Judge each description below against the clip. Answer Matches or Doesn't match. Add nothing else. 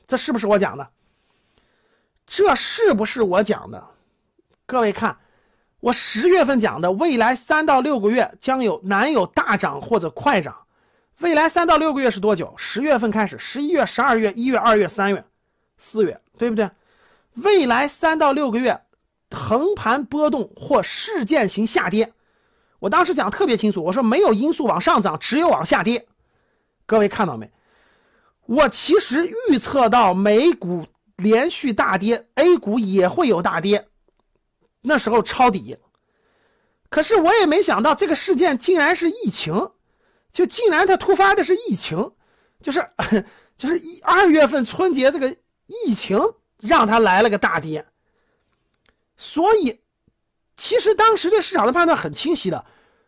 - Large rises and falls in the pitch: Matches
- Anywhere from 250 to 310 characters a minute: Doesn't match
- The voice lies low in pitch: Doesn't match